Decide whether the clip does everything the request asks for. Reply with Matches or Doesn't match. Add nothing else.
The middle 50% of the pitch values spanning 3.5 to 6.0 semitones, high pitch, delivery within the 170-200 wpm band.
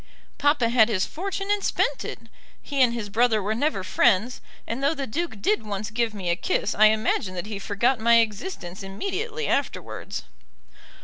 Matches